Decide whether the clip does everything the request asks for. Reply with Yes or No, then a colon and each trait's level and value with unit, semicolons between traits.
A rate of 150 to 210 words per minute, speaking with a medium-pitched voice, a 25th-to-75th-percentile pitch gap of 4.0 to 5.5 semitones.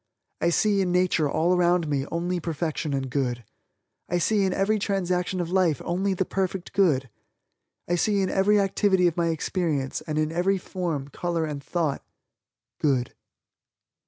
No: average, 160 wpm; medium, 175 Hz; average, 3.6 semitones